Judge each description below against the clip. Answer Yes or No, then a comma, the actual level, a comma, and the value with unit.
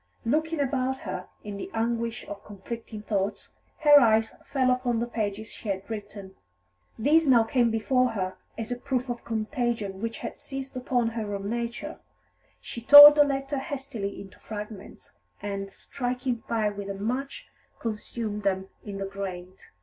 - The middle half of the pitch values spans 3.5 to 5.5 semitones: Yes, average, 3.9 semitones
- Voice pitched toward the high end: Yes, high, 230 Hz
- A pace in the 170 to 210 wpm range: No, average, 160 wpm